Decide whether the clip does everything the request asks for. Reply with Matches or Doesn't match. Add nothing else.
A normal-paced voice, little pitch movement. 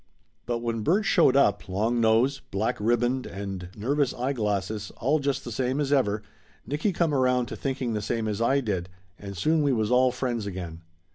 Doesn't match